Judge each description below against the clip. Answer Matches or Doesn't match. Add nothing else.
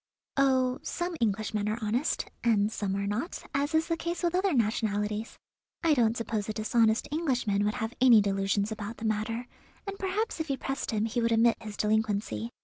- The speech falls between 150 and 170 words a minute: Doesn't match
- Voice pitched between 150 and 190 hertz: Doesn't match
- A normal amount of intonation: Matches